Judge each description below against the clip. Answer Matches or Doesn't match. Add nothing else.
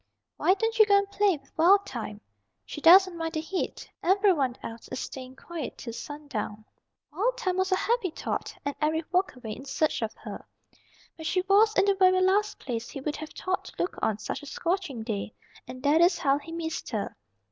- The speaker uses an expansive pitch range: Matches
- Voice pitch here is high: Matches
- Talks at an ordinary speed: Doesn't match